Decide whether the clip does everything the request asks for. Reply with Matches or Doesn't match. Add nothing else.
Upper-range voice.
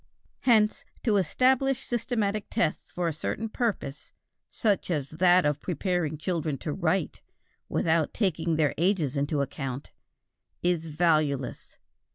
Doesn't match